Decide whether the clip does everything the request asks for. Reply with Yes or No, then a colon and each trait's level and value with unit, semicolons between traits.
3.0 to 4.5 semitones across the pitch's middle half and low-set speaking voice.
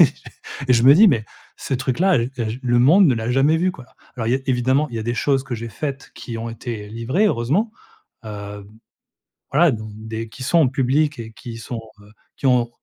Yes: average, 3.5 semitones; low, 125 Hz